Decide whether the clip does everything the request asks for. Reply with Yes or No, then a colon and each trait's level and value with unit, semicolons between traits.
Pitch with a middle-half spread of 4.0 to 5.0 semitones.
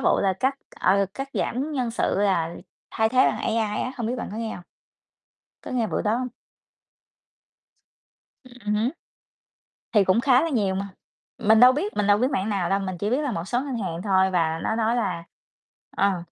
Yes: average, 4.4 semitones